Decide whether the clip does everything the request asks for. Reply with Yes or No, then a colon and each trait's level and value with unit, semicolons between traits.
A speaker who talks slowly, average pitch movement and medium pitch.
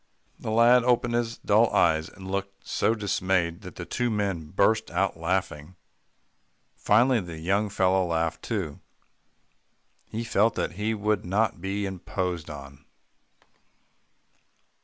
No: slow, 130 wpm; average, 4.1 semitones; very low, 95 Hz